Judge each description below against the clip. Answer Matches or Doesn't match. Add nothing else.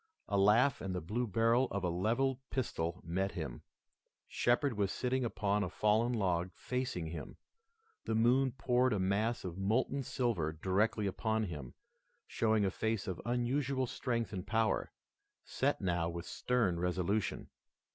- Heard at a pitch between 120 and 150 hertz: Doesn't match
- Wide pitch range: Doesn't match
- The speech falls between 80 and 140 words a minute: Doesn't match